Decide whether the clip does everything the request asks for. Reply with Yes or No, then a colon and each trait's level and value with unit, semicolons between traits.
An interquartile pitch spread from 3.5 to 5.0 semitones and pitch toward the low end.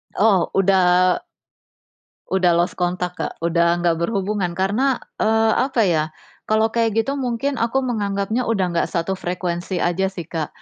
No: average, 4.1 semitones; high, 190 Hz